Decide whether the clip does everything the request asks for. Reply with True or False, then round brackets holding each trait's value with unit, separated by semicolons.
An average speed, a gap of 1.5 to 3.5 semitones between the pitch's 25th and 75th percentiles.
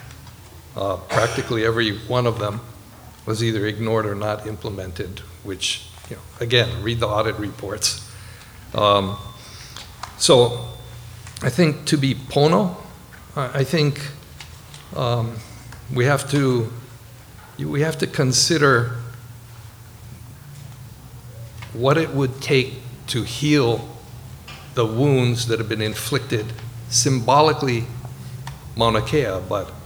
False (105 wpm; 3.1 semitones)